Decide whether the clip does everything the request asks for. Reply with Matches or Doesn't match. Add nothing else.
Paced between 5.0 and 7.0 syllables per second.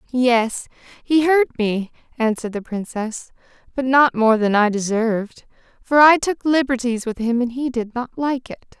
Doesn't match